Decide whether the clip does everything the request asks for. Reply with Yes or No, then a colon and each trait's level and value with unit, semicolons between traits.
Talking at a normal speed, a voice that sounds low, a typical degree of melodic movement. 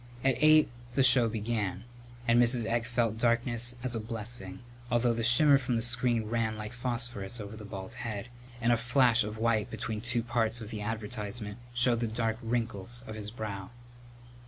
No: average, 180 wpm; low, 115 Hz; narrow, 2.0 semitones